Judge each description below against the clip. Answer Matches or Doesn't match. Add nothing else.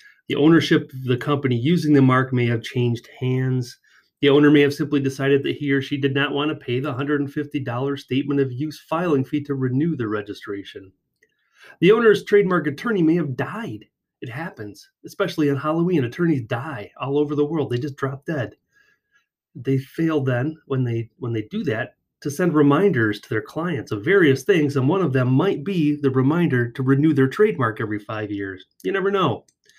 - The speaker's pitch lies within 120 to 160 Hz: Matches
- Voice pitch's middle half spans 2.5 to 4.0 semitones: Matches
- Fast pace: Doesn't match